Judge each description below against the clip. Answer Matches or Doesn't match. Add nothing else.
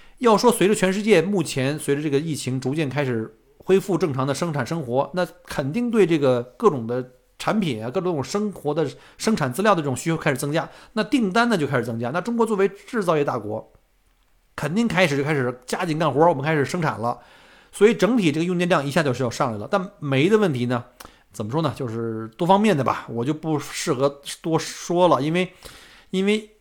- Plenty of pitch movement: Matches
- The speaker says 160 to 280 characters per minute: Doesn't match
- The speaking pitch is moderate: Matches